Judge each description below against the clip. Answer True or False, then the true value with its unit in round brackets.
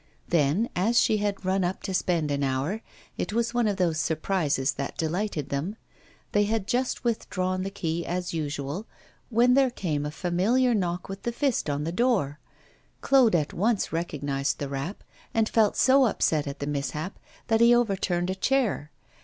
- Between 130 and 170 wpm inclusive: False (180 wpm)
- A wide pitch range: True (6.6 semitones)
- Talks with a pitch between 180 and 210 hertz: True (185 Hz)